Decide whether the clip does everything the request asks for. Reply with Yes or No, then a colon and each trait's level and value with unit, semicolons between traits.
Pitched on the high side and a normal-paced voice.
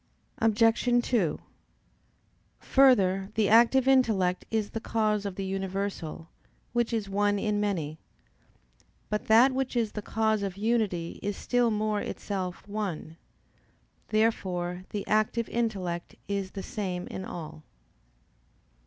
No: high, 205 Hz; slow, 125 wpm